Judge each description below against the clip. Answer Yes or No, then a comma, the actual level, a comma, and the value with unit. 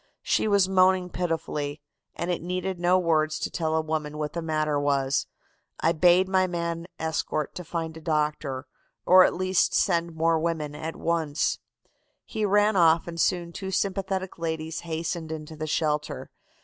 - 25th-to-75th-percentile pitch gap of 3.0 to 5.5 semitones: No, narrow, 2.6 semitones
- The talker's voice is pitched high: No, medium, 165 Hz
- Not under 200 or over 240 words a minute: No, average, 165 wpm